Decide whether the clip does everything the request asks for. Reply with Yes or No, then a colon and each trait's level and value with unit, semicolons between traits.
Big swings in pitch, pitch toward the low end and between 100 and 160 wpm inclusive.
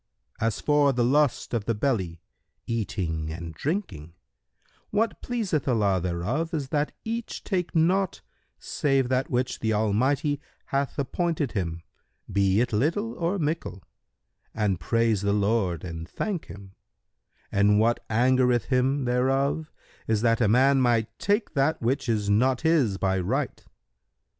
Yes: wide, 6.4 semitones; low, 125 Hz; average, 140 wpm